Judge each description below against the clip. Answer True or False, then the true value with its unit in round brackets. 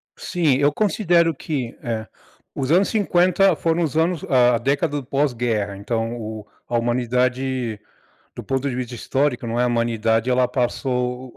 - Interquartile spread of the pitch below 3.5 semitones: False (3.8 semitones)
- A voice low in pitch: True (125 Hz)